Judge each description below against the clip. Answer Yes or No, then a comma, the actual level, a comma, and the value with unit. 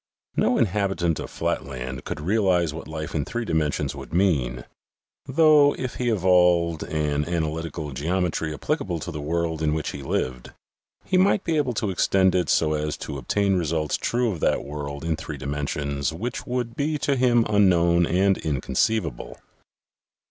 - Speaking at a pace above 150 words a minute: Yes, average, 165 wpm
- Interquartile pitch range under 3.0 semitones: No, wide, 5.4 semitones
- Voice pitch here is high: No, very low, 85 Hz